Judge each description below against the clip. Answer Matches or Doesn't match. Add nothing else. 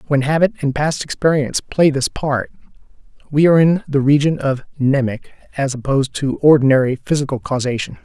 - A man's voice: Matches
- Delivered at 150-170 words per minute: Matches